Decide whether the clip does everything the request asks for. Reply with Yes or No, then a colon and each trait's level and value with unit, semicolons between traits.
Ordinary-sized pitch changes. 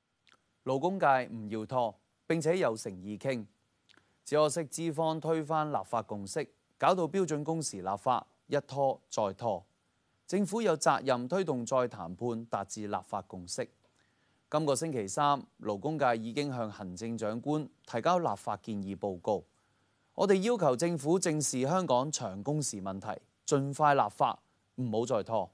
No: wide, 6.4 semitones